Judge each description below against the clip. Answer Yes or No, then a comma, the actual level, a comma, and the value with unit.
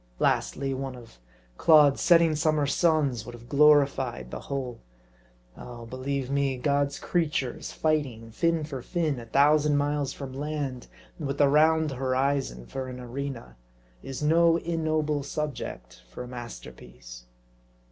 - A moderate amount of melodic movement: Yes, average, 3.2 semitones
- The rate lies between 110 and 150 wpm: Yes, slow, 135 wpm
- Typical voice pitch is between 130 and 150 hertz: Yes, medium, 140 Hz